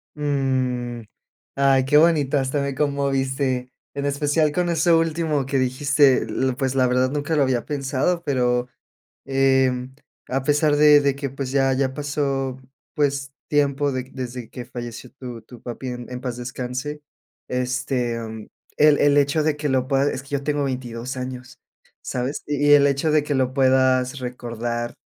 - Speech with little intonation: Yes, narrow, 2.2 semitones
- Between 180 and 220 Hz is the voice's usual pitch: No, low, 135 Hz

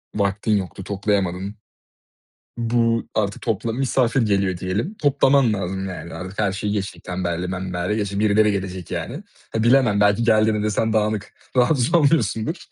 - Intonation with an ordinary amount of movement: Yes, average, 3.1 semitones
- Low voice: Yes, low, 105 Hz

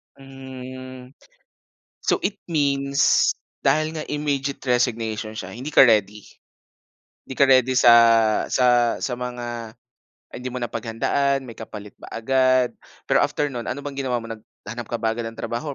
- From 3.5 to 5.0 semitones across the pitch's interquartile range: No, average, 2.7 semitones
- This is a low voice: Yes, low, 125 Hz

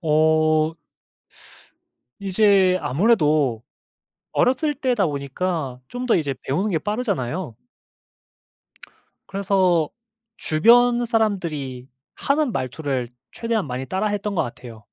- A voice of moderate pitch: Yes, medium, 175 Hz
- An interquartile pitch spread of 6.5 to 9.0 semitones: Yes, wide, 6.9 semitones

